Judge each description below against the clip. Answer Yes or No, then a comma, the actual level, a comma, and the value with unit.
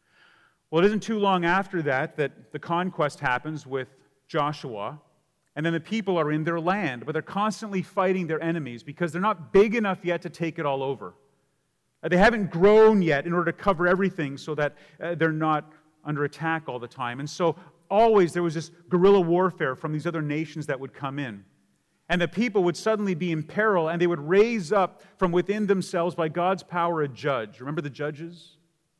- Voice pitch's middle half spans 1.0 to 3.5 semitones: No, average, 3.9 semitones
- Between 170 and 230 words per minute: Yes, average, 200 wpm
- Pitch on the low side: No, medium, 165 Hz